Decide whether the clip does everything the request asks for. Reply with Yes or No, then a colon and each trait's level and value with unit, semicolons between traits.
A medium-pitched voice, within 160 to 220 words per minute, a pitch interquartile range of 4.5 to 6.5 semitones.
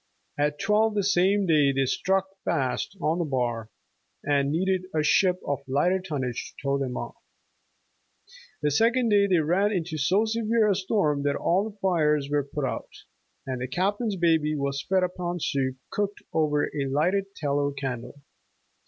Yes: medium, 160 Hz; average, 165 wpm; wide, 5.5 semitones